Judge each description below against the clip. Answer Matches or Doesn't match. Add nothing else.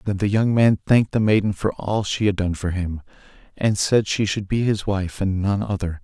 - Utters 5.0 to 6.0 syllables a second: Matches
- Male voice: Matches